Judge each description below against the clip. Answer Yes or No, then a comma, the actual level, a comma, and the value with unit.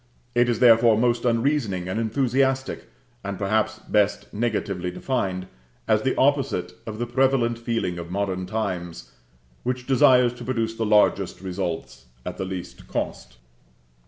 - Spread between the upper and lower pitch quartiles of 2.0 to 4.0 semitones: No, average, 4.4 semitones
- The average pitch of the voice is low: Yes, low, 110 Hz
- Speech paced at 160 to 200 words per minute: No, average, 140 wpm